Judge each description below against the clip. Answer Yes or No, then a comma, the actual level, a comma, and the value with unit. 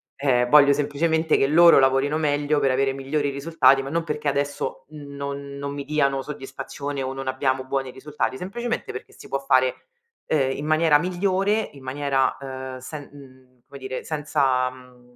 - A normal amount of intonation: No, narrow, 2.1 semitones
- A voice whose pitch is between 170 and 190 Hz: No, medium, 140 Hz